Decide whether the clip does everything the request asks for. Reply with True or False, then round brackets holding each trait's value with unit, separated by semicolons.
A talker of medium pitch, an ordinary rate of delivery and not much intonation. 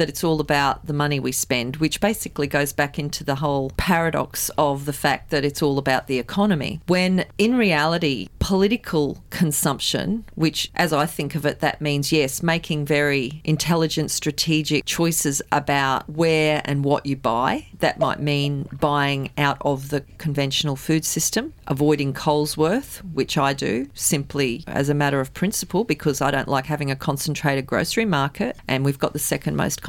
True (150 Hz; 175 wpm; 2.3 semitones)